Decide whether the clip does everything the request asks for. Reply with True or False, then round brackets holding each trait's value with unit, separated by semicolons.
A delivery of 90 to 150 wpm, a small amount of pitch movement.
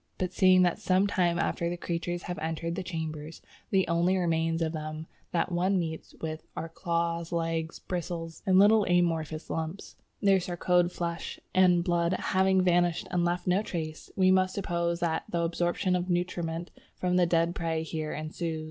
False (175 wpm; 1.8 semitones)